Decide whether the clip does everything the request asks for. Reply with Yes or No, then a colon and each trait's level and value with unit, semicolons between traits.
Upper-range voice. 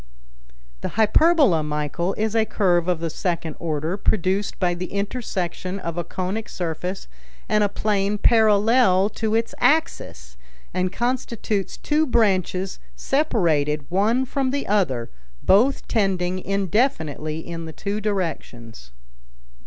Yes: high, 195 Hz